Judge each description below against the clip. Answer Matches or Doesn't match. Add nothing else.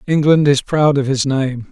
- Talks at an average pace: Doesn't match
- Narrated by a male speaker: Matches